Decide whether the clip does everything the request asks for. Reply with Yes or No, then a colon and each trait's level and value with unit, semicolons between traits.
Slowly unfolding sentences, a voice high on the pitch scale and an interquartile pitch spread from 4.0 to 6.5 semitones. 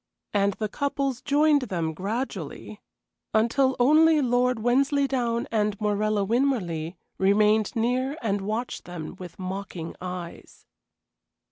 Yes: slow, 110 wpm; high, 220 Hz; average, 5.0 semitones